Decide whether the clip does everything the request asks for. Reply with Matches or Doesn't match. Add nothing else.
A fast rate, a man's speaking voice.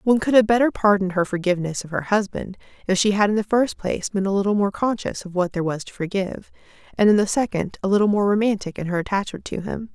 Doesn't match